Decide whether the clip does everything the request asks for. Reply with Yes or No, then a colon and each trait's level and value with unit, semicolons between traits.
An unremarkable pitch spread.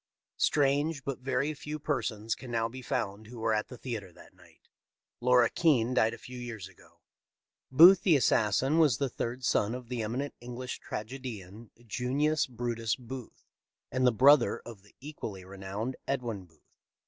Yes: average, 3.4 semitones